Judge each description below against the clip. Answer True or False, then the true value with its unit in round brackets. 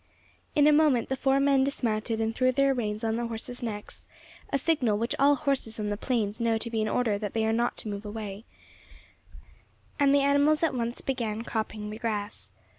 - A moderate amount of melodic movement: True (3.9 semitones)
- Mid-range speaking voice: False (230 Hz)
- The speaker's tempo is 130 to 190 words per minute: False (205 wpm)